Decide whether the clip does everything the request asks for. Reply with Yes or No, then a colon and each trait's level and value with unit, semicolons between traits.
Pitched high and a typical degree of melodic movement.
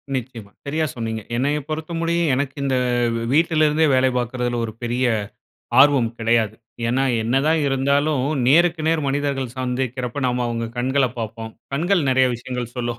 No: low, 130 Hz; average, 3.5 semitones